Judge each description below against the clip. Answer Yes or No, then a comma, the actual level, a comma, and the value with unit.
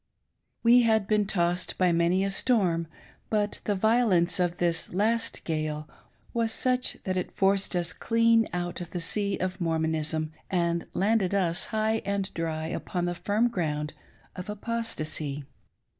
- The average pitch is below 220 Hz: Yes, medium, 185 Hz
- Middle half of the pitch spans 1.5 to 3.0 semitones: No, average, 4.2 semitones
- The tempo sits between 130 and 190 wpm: Yes, average, 150 wpm